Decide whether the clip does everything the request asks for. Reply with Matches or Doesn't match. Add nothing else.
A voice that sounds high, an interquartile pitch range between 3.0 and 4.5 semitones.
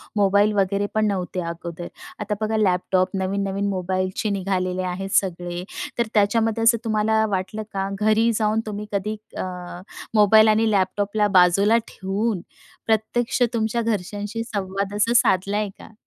Doesn't match